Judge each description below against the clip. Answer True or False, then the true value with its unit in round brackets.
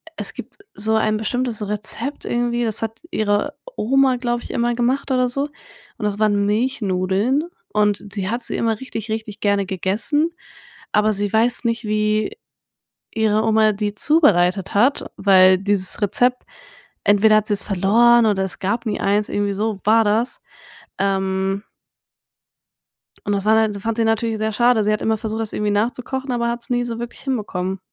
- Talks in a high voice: True (215 Hz)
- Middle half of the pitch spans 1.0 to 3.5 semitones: True (2.6 semitones)